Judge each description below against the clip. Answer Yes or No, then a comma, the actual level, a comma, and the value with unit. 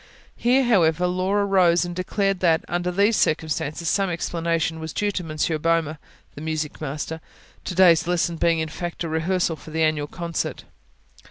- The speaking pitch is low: No, medium, 170 Hz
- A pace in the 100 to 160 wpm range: No, average, 170 wpm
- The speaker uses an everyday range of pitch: No, narrow, 2.3 semitones